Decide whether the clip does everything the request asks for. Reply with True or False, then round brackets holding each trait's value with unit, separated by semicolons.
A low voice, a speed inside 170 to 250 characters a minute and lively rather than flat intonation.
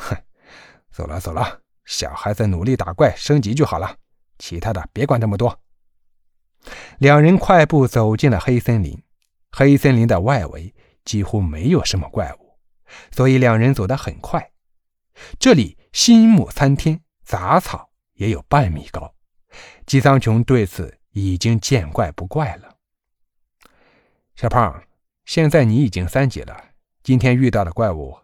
True (115 Hz; 210 characters per minute; 6.4 semitones)